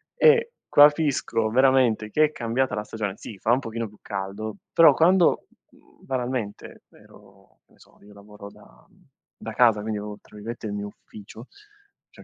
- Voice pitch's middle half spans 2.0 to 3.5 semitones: No, average, 4.2 semitones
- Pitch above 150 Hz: No, low, 110 Hz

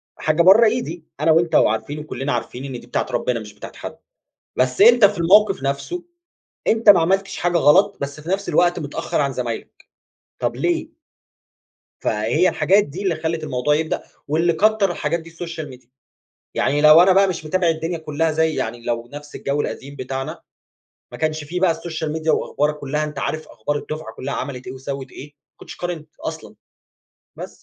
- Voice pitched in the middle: Yes, medium, 155 Hz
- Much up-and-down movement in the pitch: No, average, 3.9 semitones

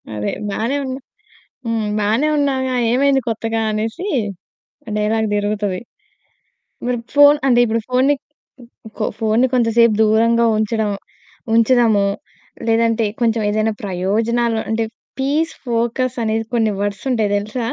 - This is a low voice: No, high, 230 Hz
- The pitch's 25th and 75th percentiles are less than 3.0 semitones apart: Yes, narrow, 2.6 semitones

